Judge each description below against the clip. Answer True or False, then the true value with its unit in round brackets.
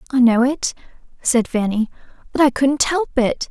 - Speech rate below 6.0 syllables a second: True (4.6 syllables/s)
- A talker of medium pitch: False (255 Hz)